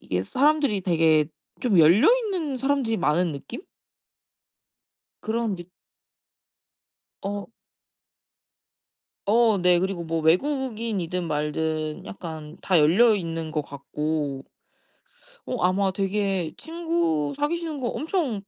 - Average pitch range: No, wide, 7.1 semitones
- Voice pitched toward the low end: No, high, 190 Hz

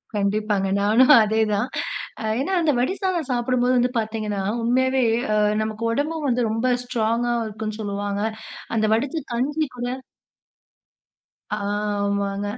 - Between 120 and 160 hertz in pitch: No, high, 225 Hz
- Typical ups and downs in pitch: Yes, average, 3.4 semitones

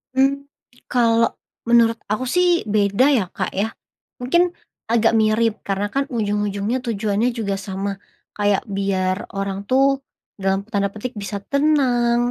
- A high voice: Yes, high, 215 Hz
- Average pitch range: Yes, average, 3.3 semitones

